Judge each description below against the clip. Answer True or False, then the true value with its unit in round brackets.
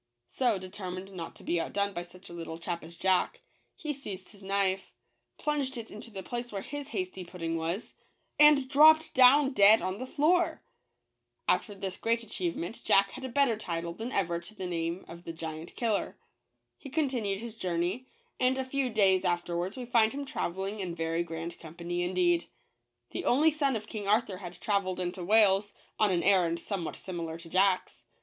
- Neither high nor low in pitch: False (195 Hz)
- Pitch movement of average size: False (5.7 semitones)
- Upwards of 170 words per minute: True (185 wpm)